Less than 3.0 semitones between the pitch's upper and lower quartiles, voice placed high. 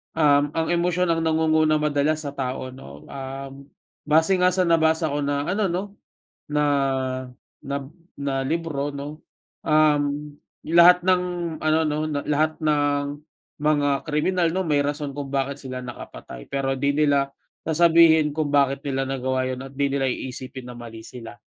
No: narrow, 2.5 semitones; medium, 145 Hz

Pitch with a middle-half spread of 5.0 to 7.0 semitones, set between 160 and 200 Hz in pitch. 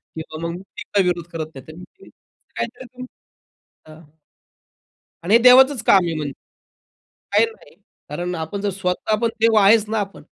Yes: wide, 5.4 semitones; high, 190 Hz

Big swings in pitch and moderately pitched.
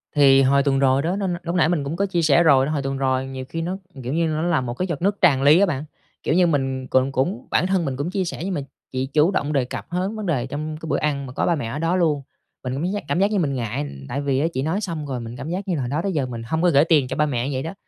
No: average, 4.5 semitones; medium, 150 Hz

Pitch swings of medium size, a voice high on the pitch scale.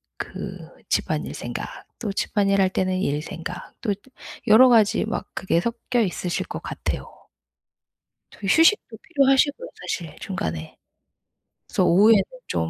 Yes: average, 5.0 semitones; high, 200 Hz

